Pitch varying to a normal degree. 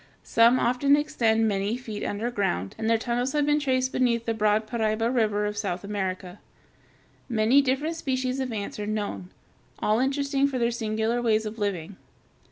Yes: average, 3.5 semitones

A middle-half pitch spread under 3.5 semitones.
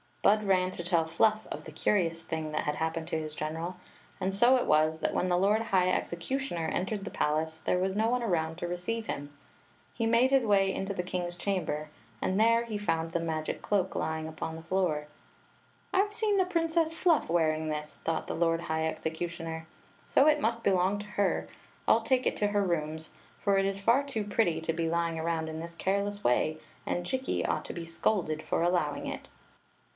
No: average, 4.6 semitones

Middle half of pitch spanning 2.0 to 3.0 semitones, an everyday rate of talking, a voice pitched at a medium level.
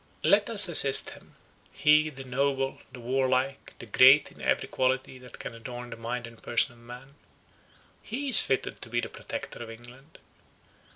No: narrow, 2.5 semitones; average, 175 wpm; low, 130 Hz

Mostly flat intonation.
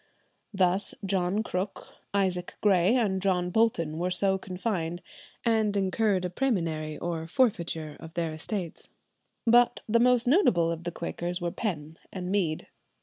No: average, 3.7 semitones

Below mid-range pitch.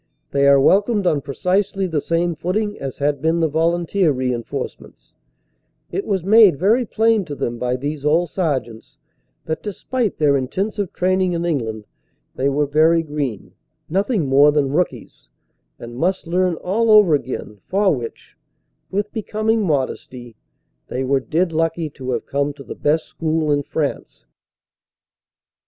No: medium, 160 Hz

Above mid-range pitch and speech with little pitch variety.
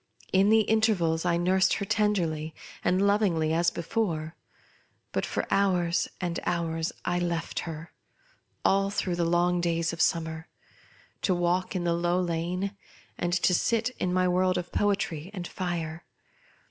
No: medium, 175 Hz; narrow, 2.1 semitones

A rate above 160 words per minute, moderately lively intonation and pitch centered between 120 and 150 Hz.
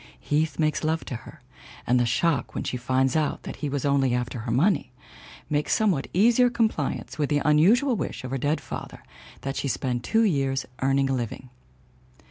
Yes: average, 190 wpm; average, 3.8 semitones; medium, 140 Hz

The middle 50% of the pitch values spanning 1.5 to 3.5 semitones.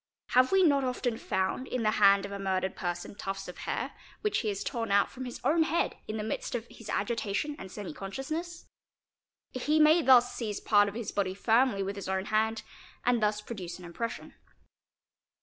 No: average, 4.4 semitones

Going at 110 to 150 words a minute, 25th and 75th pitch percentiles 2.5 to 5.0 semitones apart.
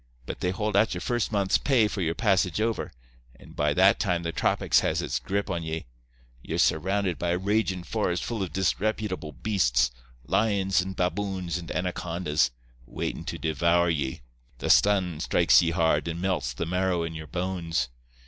No: average, 170 wpm; average, 3.4 semitones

